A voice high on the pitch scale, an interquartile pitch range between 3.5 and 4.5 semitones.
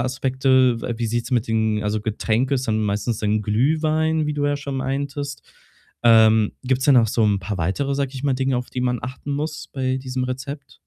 No: low, 130 Hz; average, 3.9 semitones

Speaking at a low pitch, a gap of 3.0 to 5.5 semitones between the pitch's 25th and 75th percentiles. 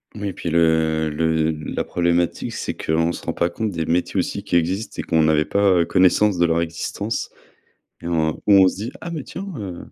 Yes: very low, 85 Hz; average, 3.5 semitones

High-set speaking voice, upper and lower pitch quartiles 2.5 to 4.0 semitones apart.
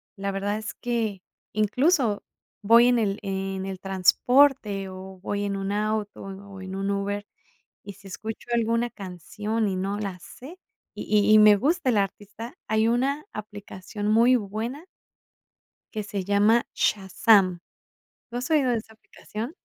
Yes: high, 210 Hz; average, 2.9 semitones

